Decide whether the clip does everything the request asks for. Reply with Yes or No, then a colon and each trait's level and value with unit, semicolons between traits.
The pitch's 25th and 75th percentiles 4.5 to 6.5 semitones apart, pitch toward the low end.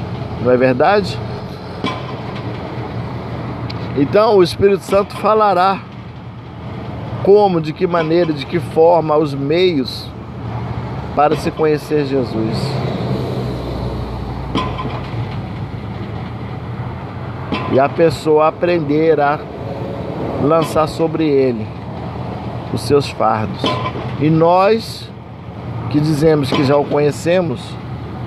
No: average, 5.1 semitones; medium, 145 Hz